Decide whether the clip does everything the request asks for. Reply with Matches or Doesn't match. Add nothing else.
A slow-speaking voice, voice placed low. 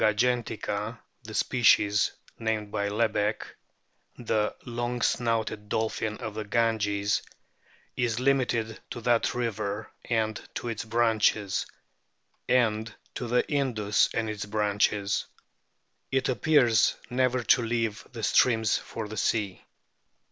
Matches